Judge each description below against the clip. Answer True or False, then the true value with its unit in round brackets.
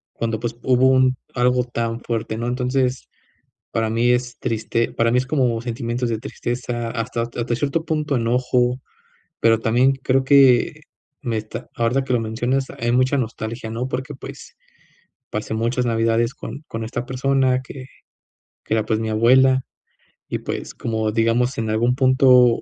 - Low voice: True (120 Hz)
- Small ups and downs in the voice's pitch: True (2.1 semitones)